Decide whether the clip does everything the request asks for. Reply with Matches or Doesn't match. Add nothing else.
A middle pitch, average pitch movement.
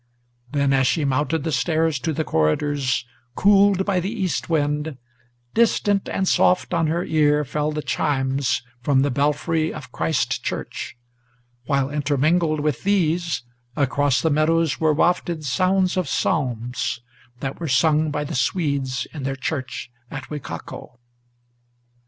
Matches